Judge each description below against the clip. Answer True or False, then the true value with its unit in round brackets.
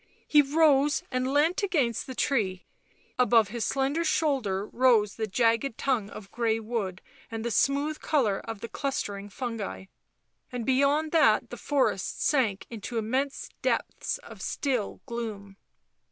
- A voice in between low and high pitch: False (240 Hz)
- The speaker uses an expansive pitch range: False (4.4 semitones)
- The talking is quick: False (140 wpm)